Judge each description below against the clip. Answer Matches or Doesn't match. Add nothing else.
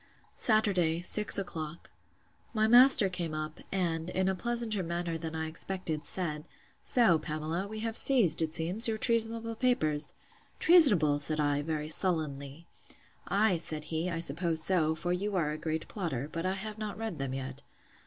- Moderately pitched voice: Matches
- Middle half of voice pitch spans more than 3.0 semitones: Matches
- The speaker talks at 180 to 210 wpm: Doesn't match